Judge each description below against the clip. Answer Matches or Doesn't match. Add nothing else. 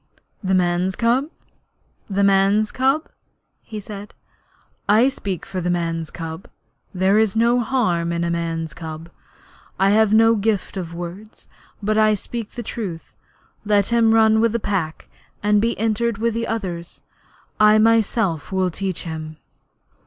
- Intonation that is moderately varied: Matches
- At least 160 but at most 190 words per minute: Doesn't match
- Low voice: Doesn't match